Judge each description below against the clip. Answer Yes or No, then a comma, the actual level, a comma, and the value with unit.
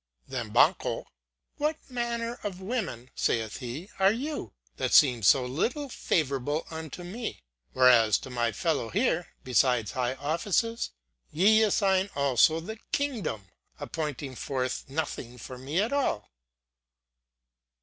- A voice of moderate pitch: Yes, medium, 155 Hz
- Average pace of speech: No, slow, 125 wpm